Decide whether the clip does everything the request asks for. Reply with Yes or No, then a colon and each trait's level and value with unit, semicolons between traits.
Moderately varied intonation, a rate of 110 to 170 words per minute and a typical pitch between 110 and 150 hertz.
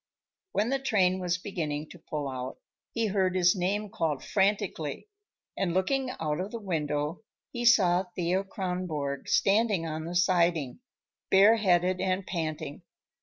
No: average, 3.7 semitones; average, 140 wpm; medium, 180 Hz